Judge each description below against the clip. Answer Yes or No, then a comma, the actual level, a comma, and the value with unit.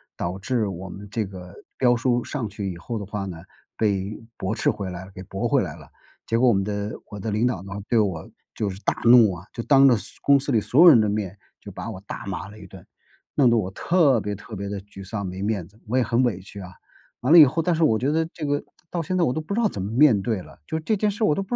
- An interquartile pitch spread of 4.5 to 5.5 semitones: Yes, average, 5.1 semitones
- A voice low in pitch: Yes, low, 110 Hz